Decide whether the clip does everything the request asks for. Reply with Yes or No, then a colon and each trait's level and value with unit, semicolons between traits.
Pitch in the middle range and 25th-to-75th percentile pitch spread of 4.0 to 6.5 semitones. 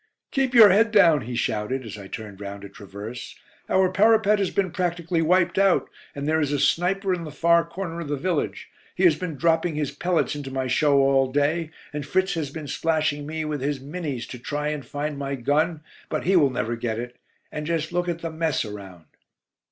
Yes: medium, 150 Hz; average, 4.5 semitones